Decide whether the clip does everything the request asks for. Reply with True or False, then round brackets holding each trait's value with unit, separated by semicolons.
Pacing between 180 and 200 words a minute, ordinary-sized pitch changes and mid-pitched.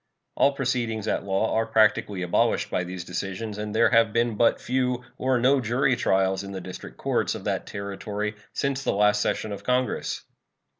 False (185 wpm; 3.9 semitones; 110 Hz)